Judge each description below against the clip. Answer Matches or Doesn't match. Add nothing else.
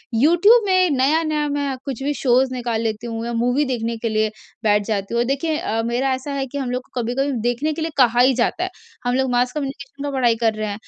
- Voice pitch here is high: Matches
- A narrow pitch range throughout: Doesn't match